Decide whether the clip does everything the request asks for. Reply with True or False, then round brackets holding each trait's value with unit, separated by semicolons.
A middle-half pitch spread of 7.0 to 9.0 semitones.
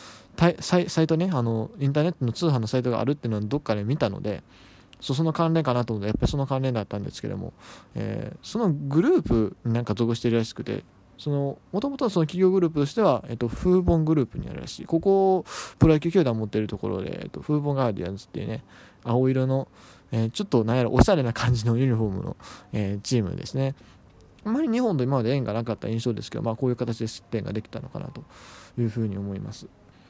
False (5.2 semitones)